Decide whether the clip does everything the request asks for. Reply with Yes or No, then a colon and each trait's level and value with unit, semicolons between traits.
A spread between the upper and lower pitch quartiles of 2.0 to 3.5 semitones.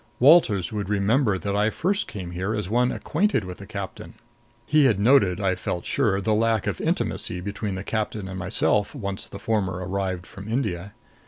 Yes: average, 3.1 semitones